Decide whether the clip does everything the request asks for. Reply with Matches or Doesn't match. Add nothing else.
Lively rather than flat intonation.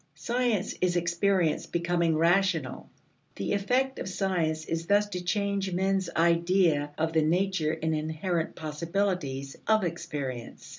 Doesn't match